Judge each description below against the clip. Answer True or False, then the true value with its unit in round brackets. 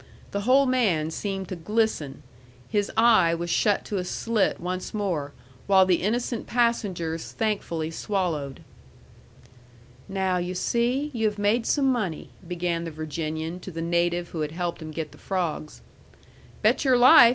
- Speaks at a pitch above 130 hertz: True (185 Hz)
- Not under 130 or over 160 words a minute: True (155 wpm)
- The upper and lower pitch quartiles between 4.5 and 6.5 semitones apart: True (4.8 semitones)